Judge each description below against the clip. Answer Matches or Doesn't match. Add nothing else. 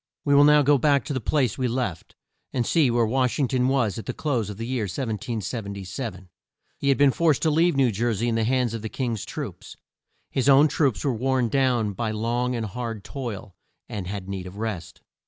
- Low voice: Matches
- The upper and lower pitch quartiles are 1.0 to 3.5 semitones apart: Doesn't match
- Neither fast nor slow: Doesn't match